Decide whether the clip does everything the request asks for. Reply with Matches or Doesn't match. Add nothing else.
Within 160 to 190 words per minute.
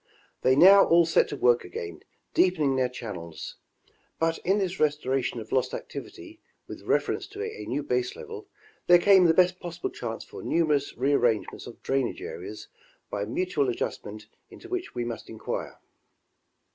Matches